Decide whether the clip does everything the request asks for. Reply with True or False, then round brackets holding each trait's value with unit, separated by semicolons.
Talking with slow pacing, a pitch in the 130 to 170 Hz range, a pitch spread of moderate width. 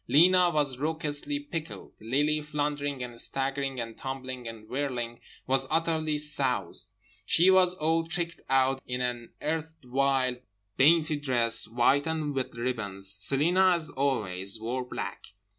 True (130 wpm; 140 Hz; 4.1 semitones)